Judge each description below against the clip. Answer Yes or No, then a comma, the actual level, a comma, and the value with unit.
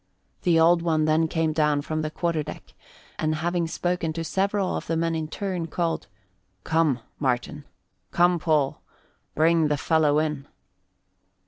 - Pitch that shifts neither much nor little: No, narrow, 1.7 semitones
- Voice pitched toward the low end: No, medium, 160 Hz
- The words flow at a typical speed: Yes, average, 150 wpm